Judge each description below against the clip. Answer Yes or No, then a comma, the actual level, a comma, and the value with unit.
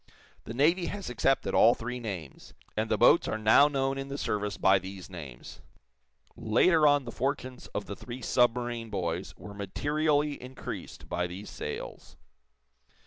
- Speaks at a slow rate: No, average, 155 wpm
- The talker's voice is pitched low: Yes, low, 120 Hz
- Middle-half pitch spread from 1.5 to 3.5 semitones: No, wide, 5.6 semitones